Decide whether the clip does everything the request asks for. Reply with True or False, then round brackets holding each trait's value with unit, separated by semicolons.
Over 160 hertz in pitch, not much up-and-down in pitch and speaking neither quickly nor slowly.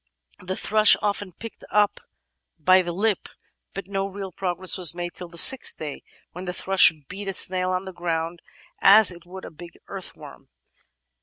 True (185 Hz; 2.0 semitones; 180 wpm)